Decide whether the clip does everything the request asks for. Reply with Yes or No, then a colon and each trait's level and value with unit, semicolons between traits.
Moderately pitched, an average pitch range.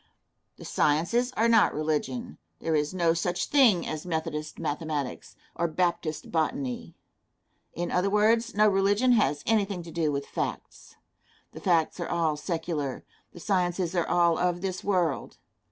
Yes: medium, 170 Hz; average, 3.8 semitones